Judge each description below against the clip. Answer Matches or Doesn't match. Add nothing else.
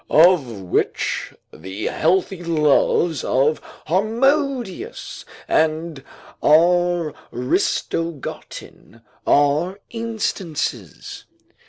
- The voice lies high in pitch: Doesn't match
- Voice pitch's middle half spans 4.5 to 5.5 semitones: Matches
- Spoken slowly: Matches